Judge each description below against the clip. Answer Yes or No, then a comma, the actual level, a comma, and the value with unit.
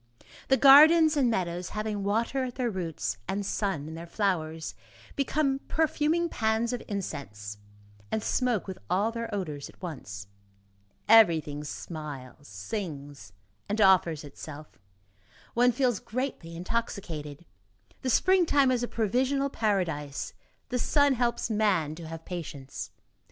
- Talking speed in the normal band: No, slow, 130 wpm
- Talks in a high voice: Yes, high, 200 Hz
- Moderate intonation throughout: No, wide, 7.8 semitones